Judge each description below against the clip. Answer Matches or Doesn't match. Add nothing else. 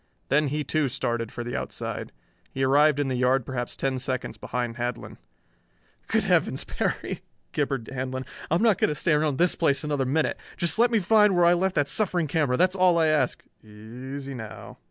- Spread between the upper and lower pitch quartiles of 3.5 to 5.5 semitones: Matches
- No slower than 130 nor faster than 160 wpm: Doesn't match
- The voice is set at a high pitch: Doesn't match